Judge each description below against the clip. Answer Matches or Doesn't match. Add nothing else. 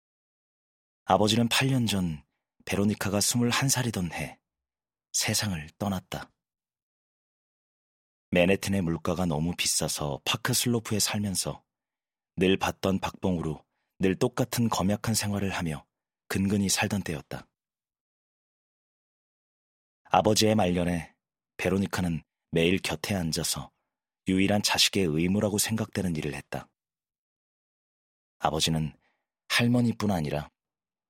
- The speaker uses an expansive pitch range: Doesn't match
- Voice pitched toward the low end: Matches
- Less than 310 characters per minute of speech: Matches